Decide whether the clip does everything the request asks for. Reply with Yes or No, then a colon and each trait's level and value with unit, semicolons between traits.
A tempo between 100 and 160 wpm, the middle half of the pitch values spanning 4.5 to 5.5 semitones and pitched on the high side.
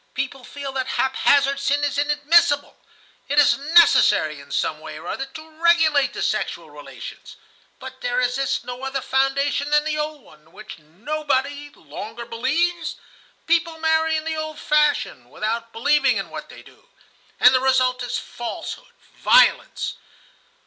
No: average, 155 wpm; average, 3.2 semitones; very high, 280 Hz